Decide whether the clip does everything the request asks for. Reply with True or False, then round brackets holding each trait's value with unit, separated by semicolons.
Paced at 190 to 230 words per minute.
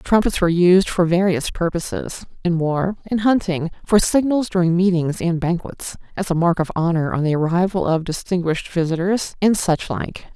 False (170 wpm)